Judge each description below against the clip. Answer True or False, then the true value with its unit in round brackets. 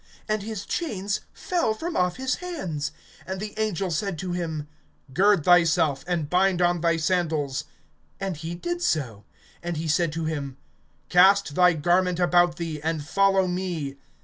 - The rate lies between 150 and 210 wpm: True (160 wpm)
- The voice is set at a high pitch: False (175 Hz)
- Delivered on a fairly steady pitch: False (3.5 semitones)